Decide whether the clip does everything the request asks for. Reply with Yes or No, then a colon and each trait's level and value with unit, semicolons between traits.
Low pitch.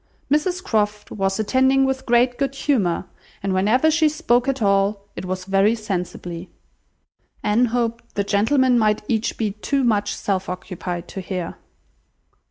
No: high, 215 Hz